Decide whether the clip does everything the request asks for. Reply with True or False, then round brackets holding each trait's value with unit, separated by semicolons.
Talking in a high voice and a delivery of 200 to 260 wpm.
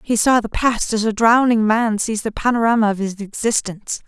True (220 Hz; 205 wpm)